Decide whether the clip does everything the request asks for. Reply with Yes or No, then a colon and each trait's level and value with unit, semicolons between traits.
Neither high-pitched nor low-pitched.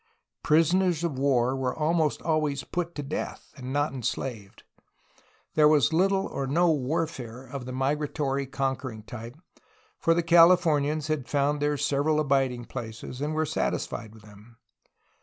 Yes: medium, 145 Hz